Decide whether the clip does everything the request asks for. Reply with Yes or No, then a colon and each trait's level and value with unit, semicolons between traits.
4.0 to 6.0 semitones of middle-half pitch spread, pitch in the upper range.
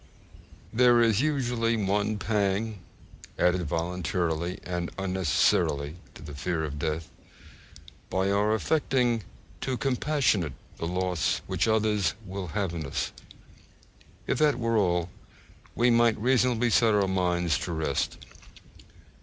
No: average, 4.9 semitones; low, 100 Hz